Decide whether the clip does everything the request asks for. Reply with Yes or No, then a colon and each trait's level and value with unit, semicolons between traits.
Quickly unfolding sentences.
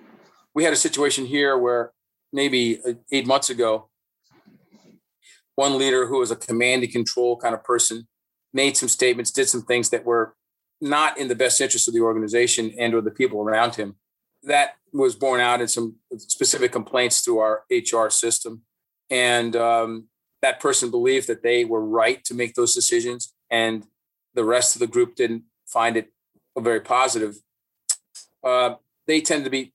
No: average, 170 wpm